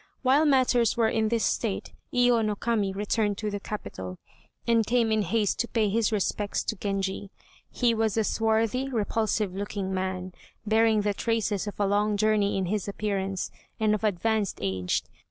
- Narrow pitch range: Yes, narrow, 2.2 semitones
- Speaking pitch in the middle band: No, high, 215 Hz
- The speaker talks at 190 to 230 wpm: No, average, 175 wpm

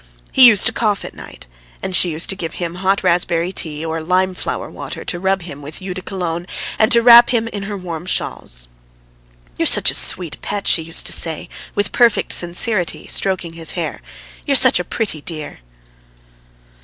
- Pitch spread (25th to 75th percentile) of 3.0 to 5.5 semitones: Yes, average, 3.6 semitones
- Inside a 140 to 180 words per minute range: No, average, 190 wpm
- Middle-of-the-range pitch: Yes, medium, 180 Hz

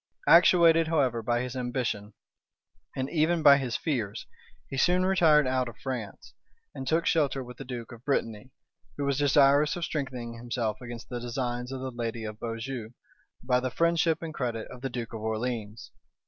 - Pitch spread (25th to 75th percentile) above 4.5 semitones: No, average, 3.6 semitones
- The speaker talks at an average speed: Yes, average, 175 wpm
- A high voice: No, low, 125 Hz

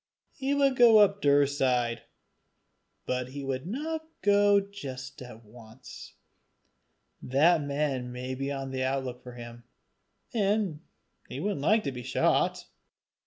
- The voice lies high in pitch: No, medium, 140 Hz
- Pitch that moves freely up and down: Yes, wide, 8.0 semitones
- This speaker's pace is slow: Yes, slow, 130 wpm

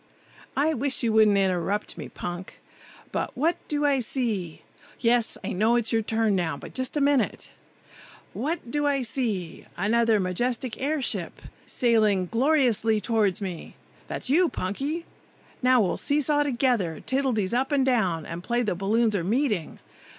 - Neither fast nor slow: Yes, average, 160 wpm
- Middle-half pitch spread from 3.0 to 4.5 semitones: No, average, 5.2 semitones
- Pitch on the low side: No, high, 235 Hz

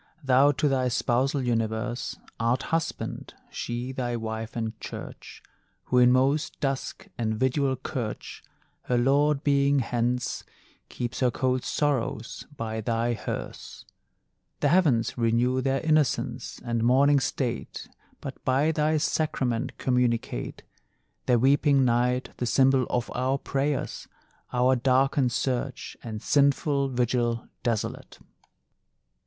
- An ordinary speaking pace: No, slow, 120 wpm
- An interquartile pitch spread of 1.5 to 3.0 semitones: Yes, narrow, 2.5 semitones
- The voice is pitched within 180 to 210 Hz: No, low, 125 Hz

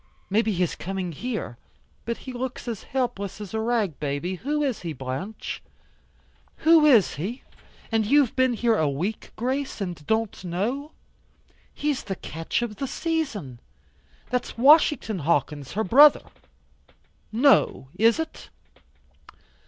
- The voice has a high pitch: Yes, high, 220 Hz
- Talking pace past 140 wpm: No, slow, 135 wpm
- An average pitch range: No, wide, 6.3 semitones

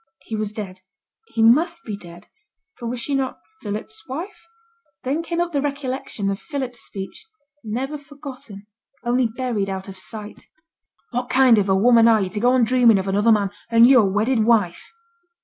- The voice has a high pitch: Yes, high, 230 Hz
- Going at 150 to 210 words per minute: Yes, average, 185 wpm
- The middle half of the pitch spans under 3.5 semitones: No, average, 4.1 semitones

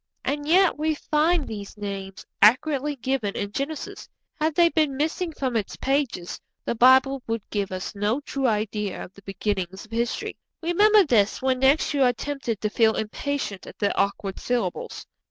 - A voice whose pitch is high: Yes, very high, 250 Hz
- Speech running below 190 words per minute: Yes, average, 170 wpm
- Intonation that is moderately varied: No, wide, 5.9 semitones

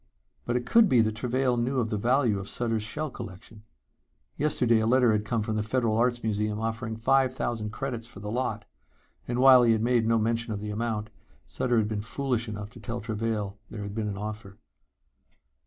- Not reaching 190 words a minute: No, fast, 205 wpm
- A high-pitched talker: No, low, 115 Hz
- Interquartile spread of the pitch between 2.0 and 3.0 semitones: Yes, narrow, 2.4 semitones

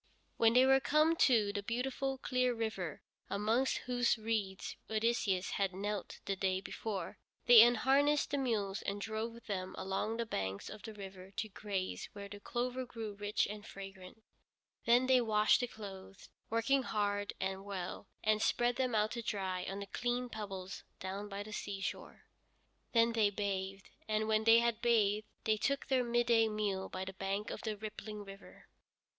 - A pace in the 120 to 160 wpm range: No, average, 170 wpm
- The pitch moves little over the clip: No, average, 3.1 semitones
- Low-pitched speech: No, high, 215 Hz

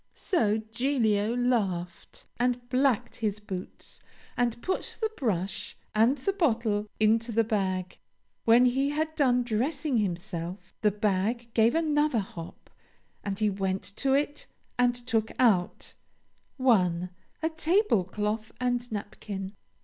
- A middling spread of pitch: Yes, average, 4.0 semitones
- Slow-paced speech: Yes, slow, 125 wpm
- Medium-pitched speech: No, high, 225 Hz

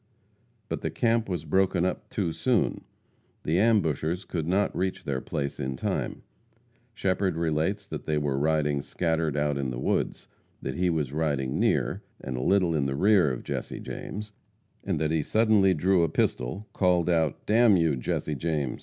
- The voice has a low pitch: Yes, very low, 80 Hz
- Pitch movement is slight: No, average, 4.7 semitones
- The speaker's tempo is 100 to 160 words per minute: No, average, 170 wpm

